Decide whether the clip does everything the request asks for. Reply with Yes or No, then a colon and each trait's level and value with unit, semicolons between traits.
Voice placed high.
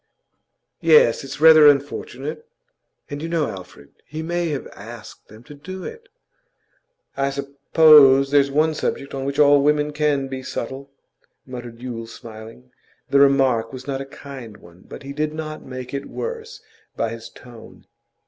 No: medium, 140 Hz